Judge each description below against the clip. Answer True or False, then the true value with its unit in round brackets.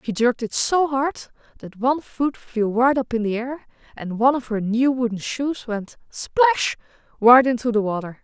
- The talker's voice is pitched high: True (245 Hz)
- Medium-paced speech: True (180 wpm)